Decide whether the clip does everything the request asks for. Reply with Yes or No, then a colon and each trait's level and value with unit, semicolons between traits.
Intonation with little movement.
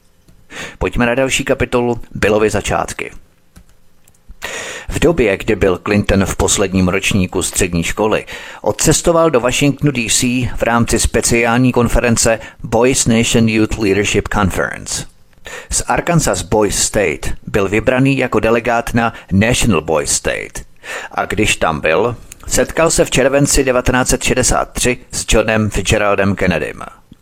No: average, 3.3 semitones